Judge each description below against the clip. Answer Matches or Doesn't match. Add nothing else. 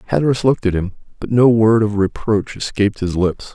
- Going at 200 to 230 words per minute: Matches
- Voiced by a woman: Doesn't match